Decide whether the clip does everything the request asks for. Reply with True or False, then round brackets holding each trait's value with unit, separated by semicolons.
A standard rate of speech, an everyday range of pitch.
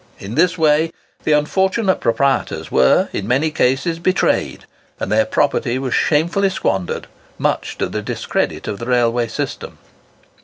False (145 wpm; 6.0 semitones)